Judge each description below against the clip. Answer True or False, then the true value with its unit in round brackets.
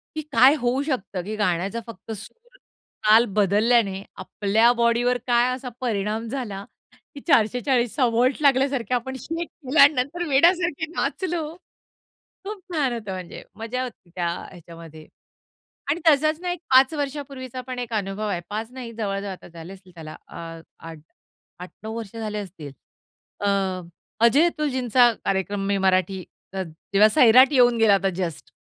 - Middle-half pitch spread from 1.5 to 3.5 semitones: False (5.1 semitones)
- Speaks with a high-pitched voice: True (230 Hz)